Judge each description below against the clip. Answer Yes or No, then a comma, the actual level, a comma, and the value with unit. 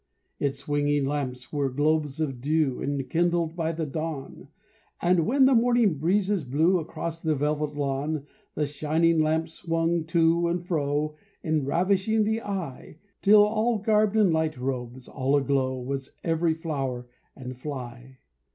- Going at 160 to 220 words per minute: No, average, 140 wpm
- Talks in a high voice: No, medium, 155 Hz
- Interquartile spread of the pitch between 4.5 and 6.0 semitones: No, average, 3.7 semitones